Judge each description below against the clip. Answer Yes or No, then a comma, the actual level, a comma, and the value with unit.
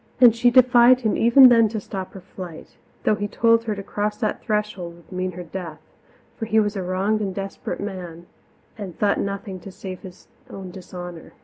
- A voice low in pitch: No, high, 200 Hz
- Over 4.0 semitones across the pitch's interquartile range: No, average, 3.0 semitones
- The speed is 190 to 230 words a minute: Yes, average, 200 wpm